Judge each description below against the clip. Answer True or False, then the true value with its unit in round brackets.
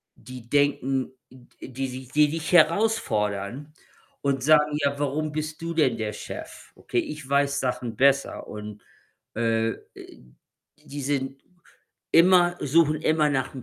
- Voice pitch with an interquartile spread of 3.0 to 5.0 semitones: True (3.3 semitones)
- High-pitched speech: False (140 Hz)